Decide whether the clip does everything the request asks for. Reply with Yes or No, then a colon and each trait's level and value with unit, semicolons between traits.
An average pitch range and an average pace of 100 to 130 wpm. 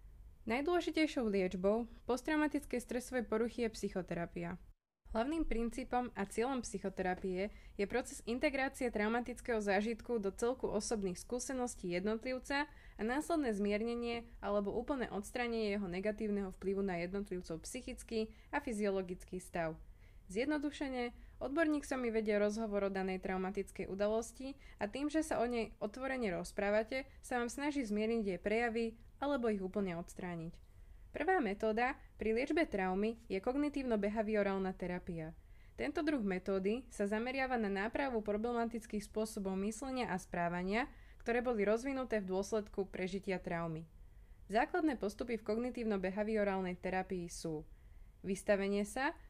Yes: average, 4.2 semitones; average, 120 wpm